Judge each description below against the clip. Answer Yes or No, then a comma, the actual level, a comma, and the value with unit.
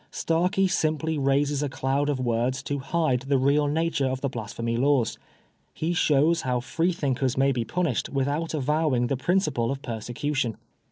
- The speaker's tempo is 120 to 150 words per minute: No, average, 165 wpm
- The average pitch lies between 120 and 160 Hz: Yes, medium, 140 Hz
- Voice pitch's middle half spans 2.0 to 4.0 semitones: Yes, average, 3.3 semitones